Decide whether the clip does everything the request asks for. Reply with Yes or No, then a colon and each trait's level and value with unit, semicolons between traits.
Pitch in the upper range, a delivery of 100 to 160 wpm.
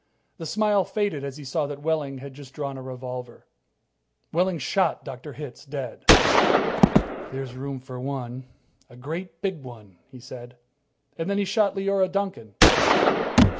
No: medium, 140 Hz; average, 150 wpm